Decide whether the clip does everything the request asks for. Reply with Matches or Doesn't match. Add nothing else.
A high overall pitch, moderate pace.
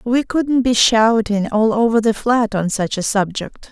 Matches